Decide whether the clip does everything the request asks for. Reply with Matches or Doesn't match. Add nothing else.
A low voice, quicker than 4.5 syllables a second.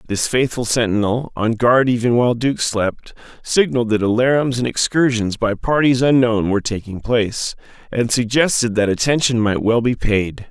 Matches